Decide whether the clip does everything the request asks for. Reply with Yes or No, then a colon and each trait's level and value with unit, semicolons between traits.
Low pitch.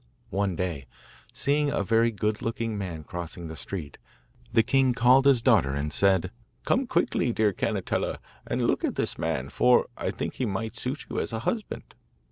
Yes: low, 110 Hz